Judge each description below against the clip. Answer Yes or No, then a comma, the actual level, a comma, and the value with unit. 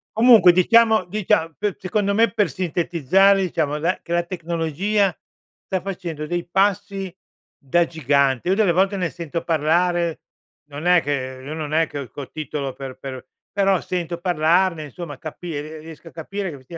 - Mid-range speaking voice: Yes, medium, 170 Hz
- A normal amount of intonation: Yes, average, 3.8 semitones